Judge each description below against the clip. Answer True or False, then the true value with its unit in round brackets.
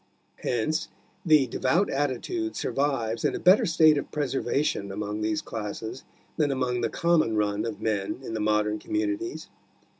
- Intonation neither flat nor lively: False (6.4 semitones)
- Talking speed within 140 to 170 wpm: True (150 wpm)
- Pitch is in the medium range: False (130 Hz)